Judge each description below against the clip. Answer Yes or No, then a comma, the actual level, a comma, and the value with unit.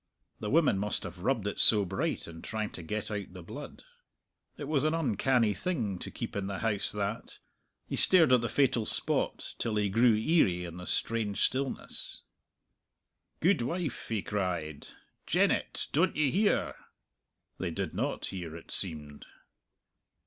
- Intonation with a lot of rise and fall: Yes, wide, 5.9 semitones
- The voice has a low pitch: Yes, low, 105 Hz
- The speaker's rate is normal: Yes, average, 155 wpm